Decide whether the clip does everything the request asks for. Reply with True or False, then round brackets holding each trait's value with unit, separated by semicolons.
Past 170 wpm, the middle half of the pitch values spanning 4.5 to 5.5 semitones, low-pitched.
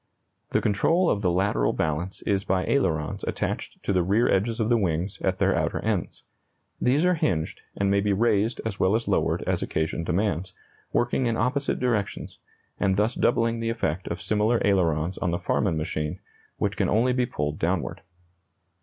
True (180 wpm; 4.9 semitones; 100 Hz)